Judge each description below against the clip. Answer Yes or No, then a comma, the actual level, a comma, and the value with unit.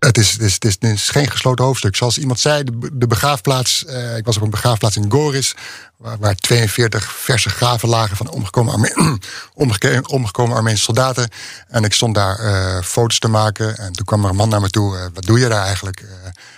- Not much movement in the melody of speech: No, average, 3.0 semitones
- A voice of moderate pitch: No, low, 115 Hz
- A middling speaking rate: No, fast, 205 wpm